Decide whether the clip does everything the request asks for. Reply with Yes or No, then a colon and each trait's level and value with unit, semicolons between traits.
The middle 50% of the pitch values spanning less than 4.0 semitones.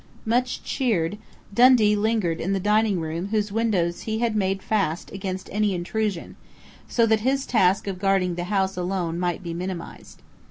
Yes: average, 3.5 semitones